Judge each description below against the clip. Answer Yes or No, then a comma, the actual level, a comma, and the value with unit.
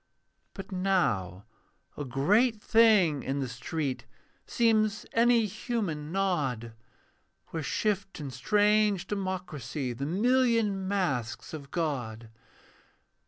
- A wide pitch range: Yes, wide, 7.5 semitones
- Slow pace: Yes, slow, 100 wpm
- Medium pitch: Yes, medium, 180 Hz